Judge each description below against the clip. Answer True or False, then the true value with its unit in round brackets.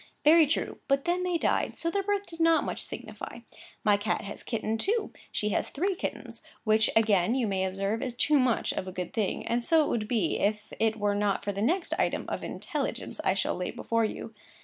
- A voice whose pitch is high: True (225 Hz)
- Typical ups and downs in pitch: False (7.8 semitones)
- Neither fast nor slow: False (225 wpm)